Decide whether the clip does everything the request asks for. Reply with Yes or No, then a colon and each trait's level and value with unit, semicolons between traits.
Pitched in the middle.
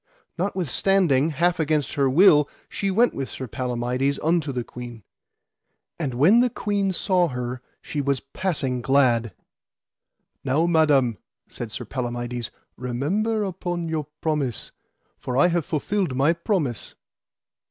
Yes: medium, 145 Hz